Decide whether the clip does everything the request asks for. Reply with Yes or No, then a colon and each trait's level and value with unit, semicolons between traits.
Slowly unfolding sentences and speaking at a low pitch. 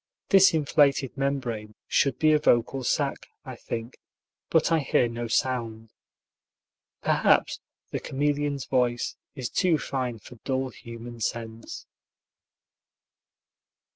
Yes: slow, 110 wpm; low, 130 Hz